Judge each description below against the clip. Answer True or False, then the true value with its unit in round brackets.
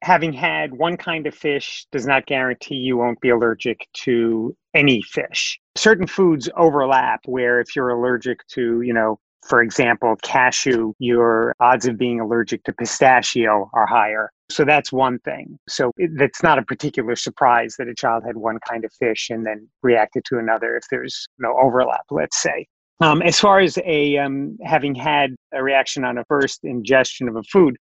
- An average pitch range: True (3.8 semitones)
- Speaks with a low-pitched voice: True (125 Hz)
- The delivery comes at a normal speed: True (185 wpm)